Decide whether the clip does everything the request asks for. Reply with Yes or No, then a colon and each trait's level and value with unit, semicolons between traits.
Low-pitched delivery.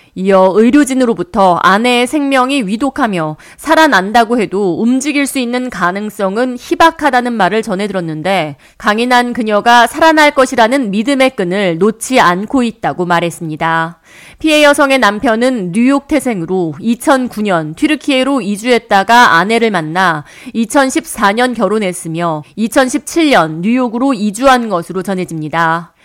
No: high, 230 Hz